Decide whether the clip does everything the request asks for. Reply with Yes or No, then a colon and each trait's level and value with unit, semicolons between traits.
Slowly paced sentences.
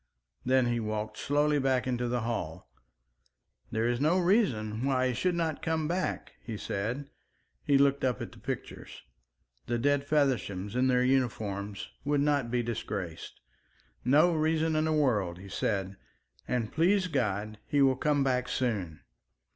No: average, 155 wpm